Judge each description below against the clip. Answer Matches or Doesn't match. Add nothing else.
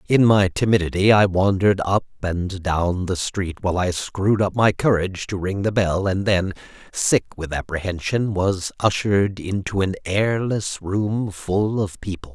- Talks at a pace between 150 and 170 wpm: Matches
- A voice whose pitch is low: Matches